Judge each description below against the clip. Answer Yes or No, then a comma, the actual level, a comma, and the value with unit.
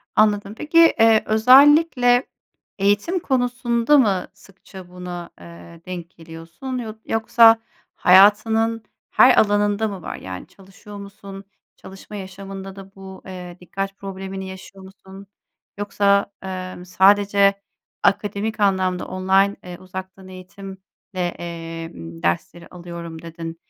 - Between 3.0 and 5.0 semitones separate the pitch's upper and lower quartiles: No, narrow, 2.4 semitones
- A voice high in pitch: Yes, high, 195 Hz